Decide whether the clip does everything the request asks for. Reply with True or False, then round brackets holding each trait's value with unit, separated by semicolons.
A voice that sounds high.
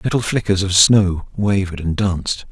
False (95 Hz)